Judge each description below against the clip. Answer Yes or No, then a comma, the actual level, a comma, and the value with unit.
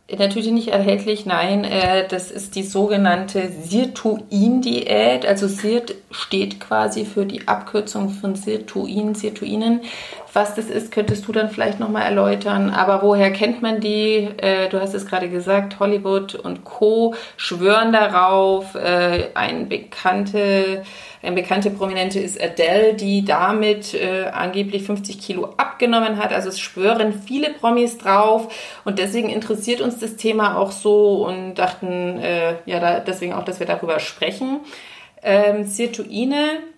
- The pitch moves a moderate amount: No, narrow, 2.1 semitones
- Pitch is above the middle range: Yes, high, 205 Hz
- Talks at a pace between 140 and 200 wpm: No, average, 130 wpm